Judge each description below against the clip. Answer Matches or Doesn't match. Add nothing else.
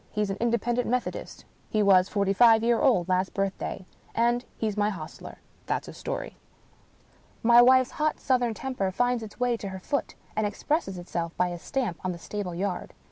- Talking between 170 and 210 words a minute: Matches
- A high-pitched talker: Matches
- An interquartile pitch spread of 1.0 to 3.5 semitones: Doesn't match